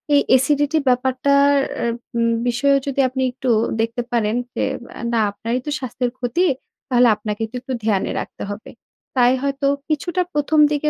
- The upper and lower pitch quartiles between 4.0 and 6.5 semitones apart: No, average, 3.0 semitones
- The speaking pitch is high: Yes, very high, 255 Hz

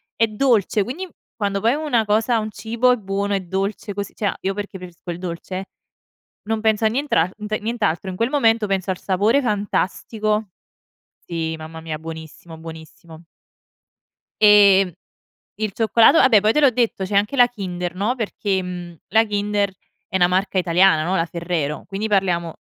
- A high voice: Yes, high, 200 Hz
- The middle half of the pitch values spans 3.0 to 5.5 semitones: Yes, average, 3.6 semitones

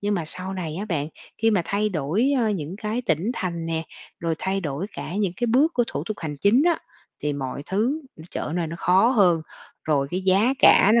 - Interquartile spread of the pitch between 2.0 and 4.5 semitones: No, average, 4.9 semitones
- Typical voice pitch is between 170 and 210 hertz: Yes, high, 190 Hz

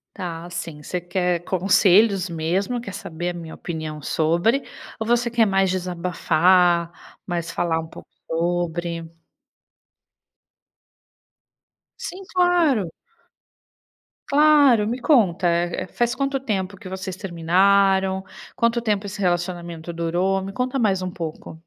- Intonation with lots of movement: No, average, 3.7 semitones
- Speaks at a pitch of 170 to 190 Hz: Yes, medium, 185 Hz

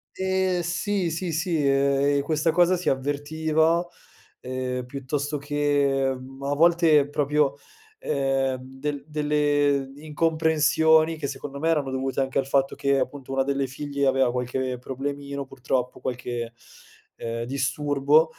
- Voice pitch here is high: No, medium, 140 Hz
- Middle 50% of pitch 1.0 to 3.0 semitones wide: Yes, narrow, 2.6 semitones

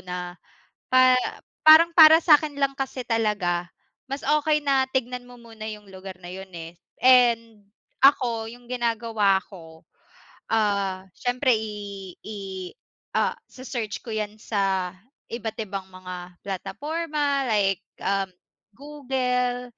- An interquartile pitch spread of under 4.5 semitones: No, average, 5.0 semitones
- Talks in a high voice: Yes, high, 225 Hz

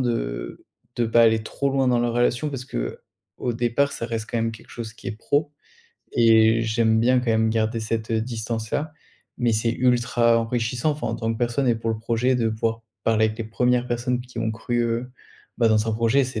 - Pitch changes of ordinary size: No, narrow, 1.6 semitones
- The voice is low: Yes, low, 115 Hz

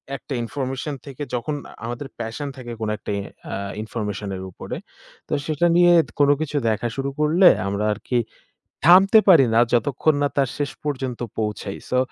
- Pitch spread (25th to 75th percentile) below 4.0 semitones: No, average, 4.4 semitones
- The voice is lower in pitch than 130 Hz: No, low, 135 Hz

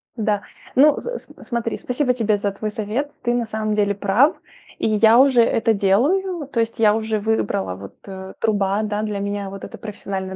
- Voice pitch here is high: Yes, high, 215 Hz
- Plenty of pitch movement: No, average, 2.9 semitones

